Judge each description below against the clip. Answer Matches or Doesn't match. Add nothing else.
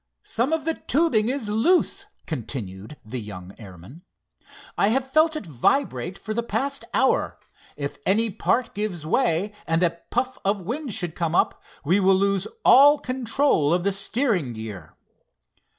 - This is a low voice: Doesn't match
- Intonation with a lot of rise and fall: Matches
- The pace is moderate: Matches